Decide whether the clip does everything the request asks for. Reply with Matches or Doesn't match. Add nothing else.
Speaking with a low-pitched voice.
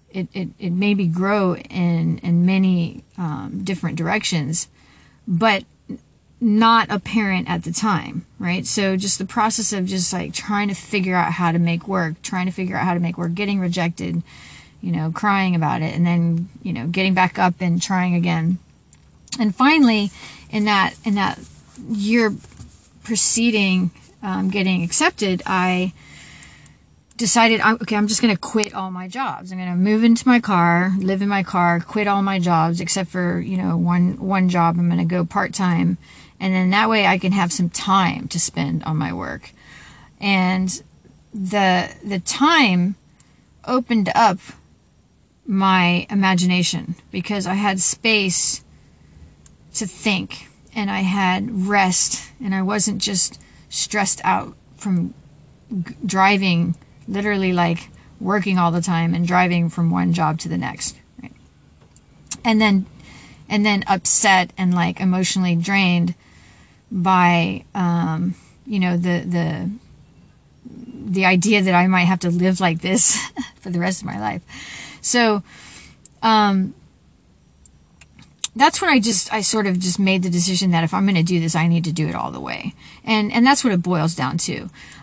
Doesn't match